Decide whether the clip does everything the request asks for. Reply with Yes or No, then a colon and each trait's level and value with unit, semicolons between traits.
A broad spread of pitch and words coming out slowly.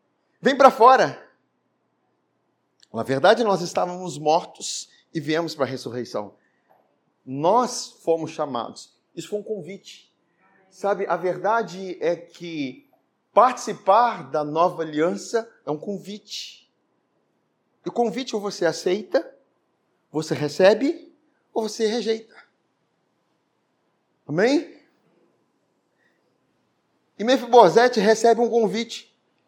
Yes: wide, 5.7 semitones; slow, 100 wpm